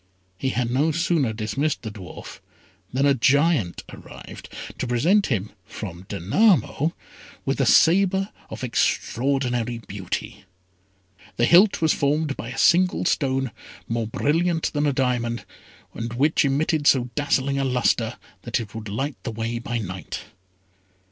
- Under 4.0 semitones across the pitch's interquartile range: No, average, 4.7 semitones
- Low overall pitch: Yes, low, 130 Hz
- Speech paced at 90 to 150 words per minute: Yes, average, 140 wpm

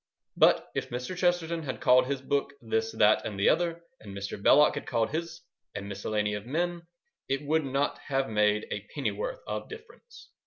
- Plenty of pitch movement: Yes, wide, 7.7 semitones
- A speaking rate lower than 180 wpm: No, average, 185 wpm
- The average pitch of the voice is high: No, low, 135 Hz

